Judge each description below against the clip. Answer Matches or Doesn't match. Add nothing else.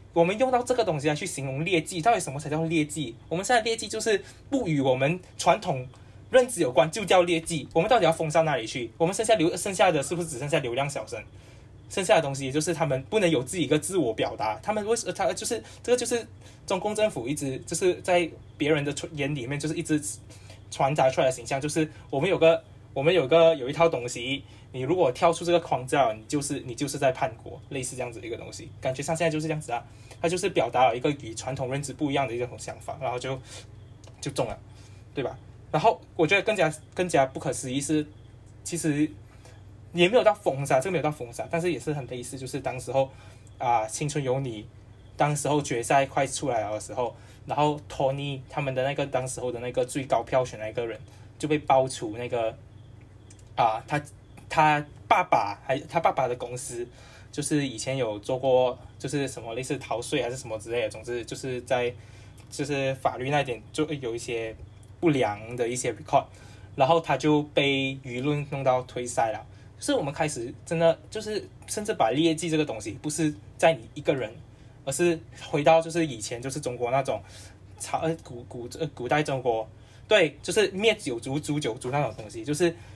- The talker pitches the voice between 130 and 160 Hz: Matches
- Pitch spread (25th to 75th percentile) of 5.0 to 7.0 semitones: Matches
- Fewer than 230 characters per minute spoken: Doesn't match